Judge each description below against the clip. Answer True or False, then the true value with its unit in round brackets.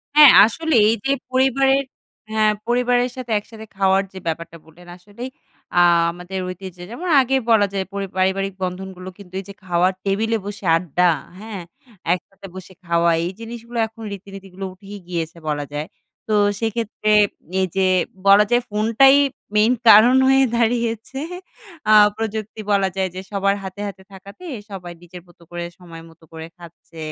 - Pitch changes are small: False (3.9 semitones)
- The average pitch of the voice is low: False (195 Hz)